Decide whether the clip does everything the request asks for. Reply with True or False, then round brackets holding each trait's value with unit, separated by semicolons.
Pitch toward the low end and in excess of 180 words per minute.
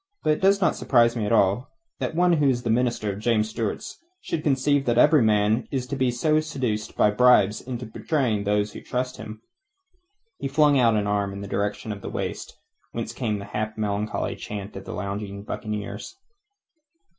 True (115 Hz; 190 wpm)